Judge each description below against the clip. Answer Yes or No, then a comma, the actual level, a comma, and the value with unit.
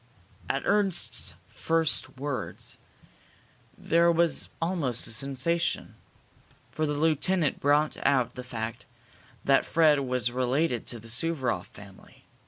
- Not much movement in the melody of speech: No, average, 4.7 semitones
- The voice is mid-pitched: Yes, medium, 145 Hz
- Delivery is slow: Yes, slow, 115 wpm